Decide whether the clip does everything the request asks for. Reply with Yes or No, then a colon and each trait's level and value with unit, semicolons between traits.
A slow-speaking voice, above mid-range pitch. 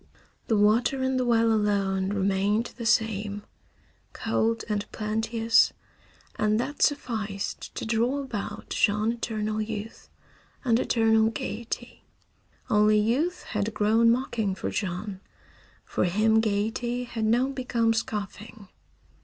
Yes: slow, 120 wpm; high, 220 Hz